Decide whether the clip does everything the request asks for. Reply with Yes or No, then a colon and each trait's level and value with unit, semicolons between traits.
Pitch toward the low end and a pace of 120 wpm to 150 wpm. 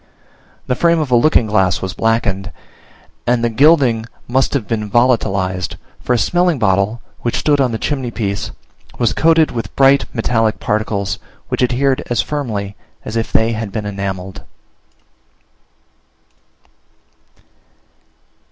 Yes: low, 115 Hz; slow, 135 wpm